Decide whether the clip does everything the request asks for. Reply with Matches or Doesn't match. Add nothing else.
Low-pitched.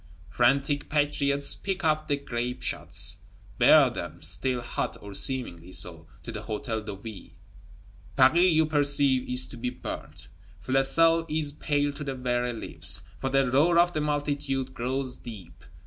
Matches